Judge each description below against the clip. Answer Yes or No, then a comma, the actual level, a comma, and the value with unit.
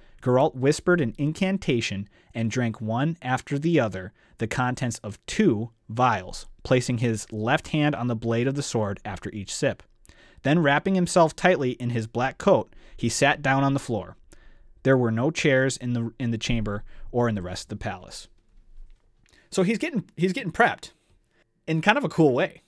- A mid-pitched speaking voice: No, low, 120 Hz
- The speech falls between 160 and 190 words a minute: Yes, average, 185 wpm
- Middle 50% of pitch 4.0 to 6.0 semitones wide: Yes, average, 4.5 semitones